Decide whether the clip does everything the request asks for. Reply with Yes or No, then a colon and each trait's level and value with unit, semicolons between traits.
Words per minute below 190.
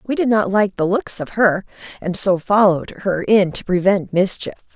No: average, 200 wpm